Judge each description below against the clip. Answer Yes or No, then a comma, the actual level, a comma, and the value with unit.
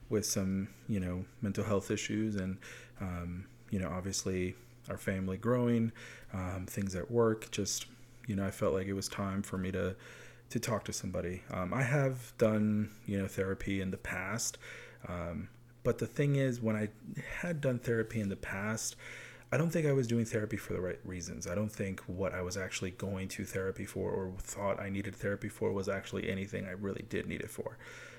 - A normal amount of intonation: Yes, average, 3.4 semitones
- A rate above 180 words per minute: Yes, average, 200 wpm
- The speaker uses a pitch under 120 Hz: Yes, low, 100 Hz